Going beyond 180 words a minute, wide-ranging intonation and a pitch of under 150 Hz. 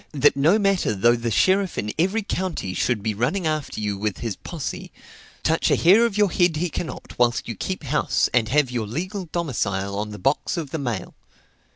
Yes: fast, 205 wpm; wide, 8.3 semitones; medium, 140 Hz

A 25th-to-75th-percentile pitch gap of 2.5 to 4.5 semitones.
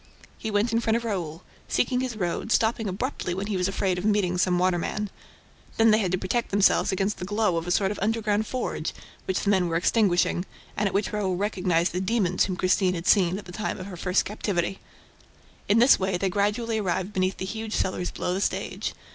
Yes: average, 2.8 semitones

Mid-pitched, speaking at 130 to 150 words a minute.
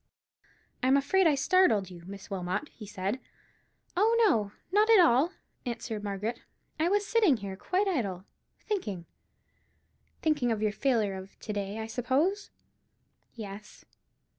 No: high, 235 Hz; average, 140 wpm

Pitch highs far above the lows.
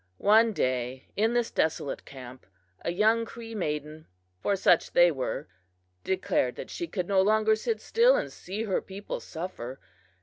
Yes: wide, 6.5 semitones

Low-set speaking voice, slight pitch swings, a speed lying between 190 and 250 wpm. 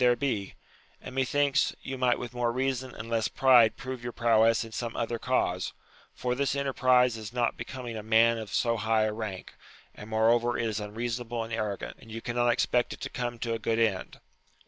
Yes: low, 120 Hz; narrow, 2.0 semitones; fast, 205 wpm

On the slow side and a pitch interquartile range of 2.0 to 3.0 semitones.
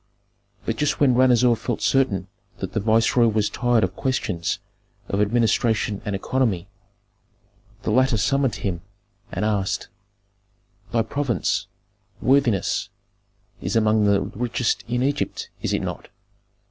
No: slow, 125 wpm; average, 3.5 semitones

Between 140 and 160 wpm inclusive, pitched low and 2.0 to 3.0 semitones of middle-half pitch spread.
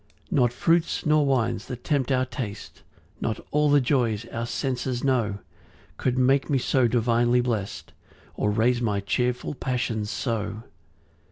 Yes: average, 150 wpm; low, 125 Hz; average, 2.7 semitones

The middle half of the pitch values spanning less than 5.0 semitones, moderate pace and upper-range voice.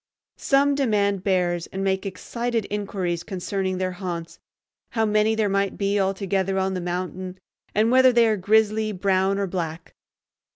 Yes: narrow, 2.5 semitones; average, 155 wpm; high, 195 Hz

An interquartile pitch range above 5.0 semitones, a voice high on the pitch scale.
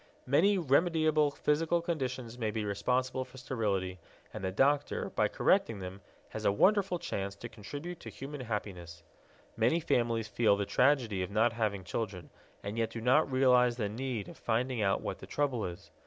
No: wide, 5.4 semitones; low, 120 Hz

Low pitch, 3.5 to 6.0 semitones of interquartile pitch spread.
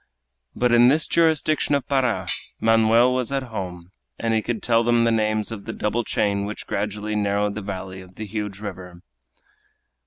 No: low, 110 Hz; average, 2.9 semitones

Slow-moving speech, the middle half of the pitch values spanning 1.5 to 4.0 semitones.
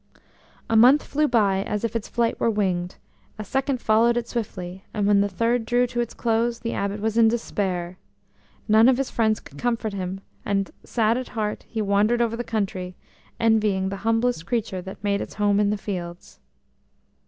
No: average, 190 wpm; average, 2.8 semitones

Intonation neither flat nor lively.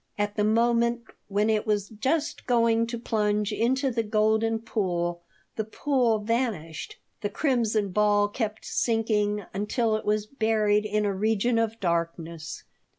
No: narrow, 1.9 semitones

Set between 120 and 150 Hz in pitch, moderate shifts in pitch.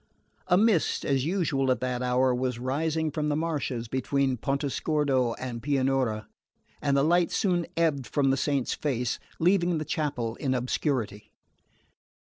Yes: medium, 140 Hz; average, 3.6 semitones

